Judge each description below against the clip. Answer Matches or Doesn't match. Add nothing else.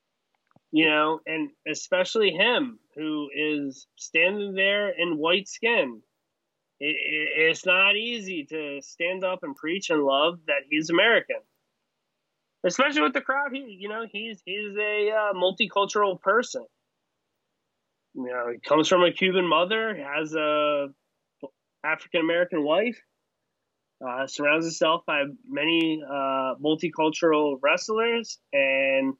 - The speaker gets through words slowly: Matches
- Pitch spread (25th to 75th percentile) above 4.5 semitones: Matches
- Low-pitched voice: Doesn't match